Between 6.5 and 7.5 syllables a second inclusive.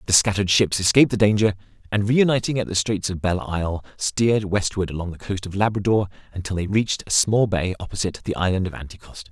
Yes: 6.6 syllables/s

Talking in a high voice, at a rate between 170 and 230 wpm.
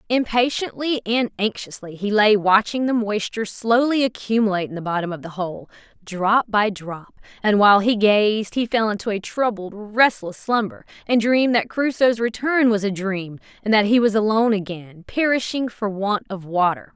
Yes: high, 215 Hz; average, 175 wpm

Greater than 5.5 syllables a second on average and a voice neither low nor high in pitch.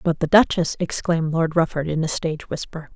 Yes: 5.7 syllables/s; medium, 165 Hz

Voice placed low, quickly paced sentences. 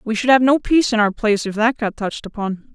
No: high, 225 Hz; fast, 285 wpm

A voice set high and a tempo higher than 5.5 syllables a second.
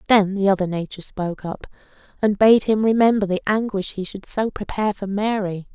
Yes: high, 200 Hz; 5.7 syllables/s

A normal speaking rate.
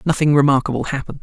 Yes: average, 145 wpm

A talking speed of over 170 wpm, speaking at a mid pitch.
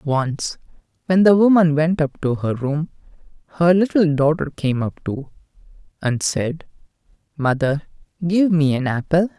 No: average, 140 wpm; medium, 155 Hz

